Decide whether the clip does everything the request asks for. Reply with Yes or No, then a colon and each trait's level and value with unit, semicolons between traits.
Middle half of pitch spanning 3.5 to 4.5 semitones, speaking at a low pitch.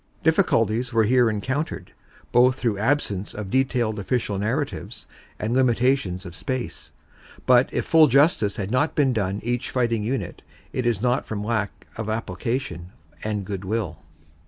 Yes: average, 3.9 semitones; low, 115 Hz